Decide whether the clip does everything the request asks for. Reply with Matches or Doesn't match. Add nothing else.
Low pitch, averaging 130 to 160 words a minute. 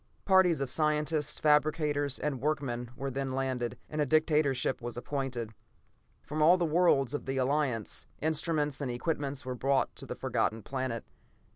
Doesn't match